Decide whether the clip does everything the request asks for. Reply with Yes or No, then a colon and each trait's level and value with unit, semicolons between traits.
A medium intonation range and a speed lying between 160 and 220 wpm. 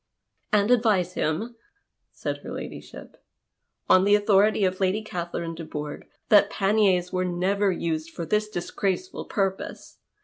No: average, 3.1 semitones; average, 145 wpm